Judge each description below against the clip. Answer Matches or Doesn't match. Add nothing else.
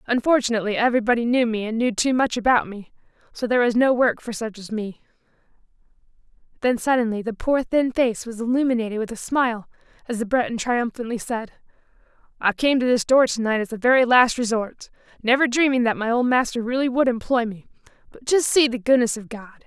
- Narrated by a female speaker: Matches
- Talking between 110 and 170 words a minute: Doesn't match